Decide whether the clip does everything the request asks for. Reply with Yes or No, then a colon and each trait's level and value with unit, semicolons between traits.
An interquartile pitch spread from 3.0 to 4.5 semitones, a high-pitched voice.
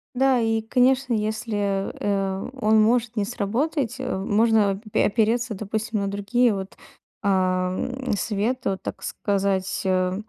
Yes: average, 3.3 semitones; high, 215 Hz